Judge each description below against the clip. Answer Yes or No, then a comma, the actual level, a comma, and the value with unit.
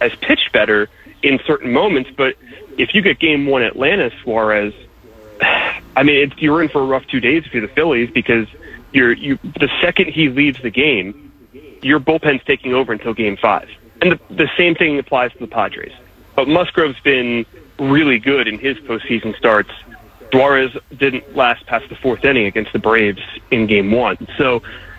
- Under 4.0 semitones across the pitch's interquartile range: No, average, 4.6 semitones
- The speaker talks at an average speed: Yes, average, 185 wpm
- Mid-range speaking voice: No, low, 130 Hz